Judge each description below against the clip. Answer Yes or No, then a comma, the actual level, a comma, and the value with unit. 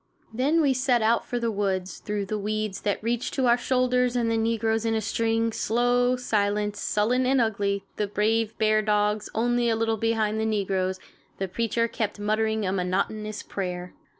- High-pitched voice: Yes, high, 220 Hz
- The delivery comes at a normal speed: Yes, average, 175 wpm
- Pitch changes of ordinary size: No, narrow, 2.2 semitones